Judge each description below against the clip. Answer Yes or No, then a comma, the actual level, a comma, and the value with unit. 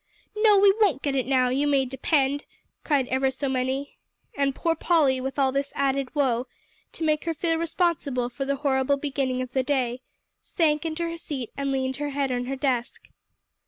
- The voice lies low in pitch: No, very high, 275 Hz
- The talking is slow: No, average, 195 wpm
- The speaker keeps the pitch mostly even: Yes, narrow, 2.3 semitones